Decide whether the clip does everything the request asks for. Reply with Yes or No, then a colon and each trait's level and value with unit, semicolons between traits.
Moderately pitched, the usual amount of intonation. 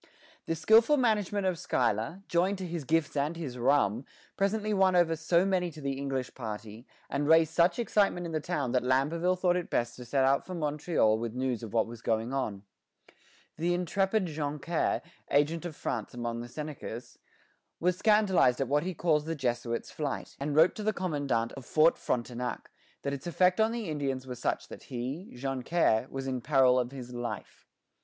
No: medium, 150 Hz; wide, 5.8 semitones